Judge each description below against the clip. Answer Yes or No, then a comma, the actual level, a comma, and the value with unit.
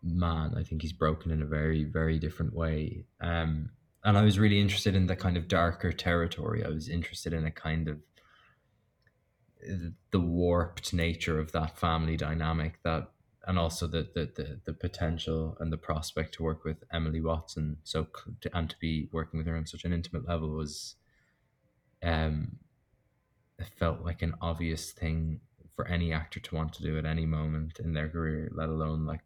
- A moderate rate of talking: Yes, average, 185 wpm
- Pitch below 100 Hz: Yes, very low, 80 Hz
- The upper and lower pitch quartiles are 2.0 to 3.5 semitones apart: Yes, narrow, 2.4 semitones